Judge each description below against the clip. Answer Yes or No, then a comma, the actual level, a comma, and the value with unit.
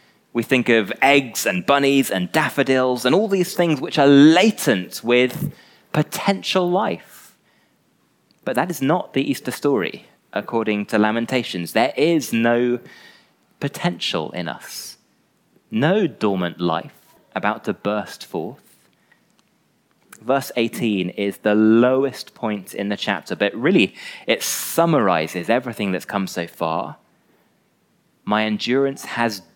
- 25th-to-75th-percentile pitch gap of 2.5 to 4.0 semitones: No, average, 5.0 semitones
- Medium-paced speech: No, slow, 125 wpm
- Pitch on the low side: Yes, low, 125 Hz